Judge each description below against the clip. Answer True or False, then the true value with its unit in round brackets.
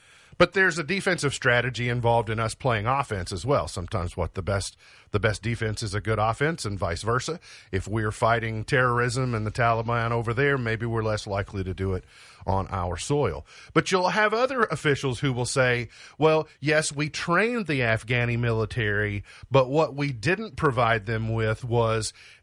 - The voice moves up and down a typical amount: True (4.7 semitones)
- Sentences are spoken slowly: False (185 wpm)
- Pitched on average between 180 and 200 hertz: False (120 Hz)